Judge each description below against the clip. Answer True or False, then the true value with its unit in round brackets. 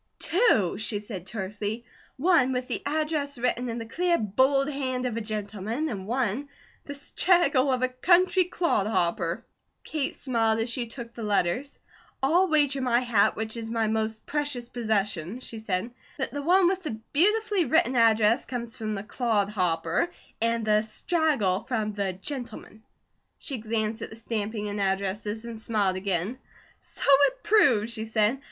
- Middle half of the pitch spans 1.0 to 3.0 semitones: False (4.5 semitones)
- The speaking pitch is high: True (230 Hz)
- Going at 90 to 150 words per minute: False (165 wpm)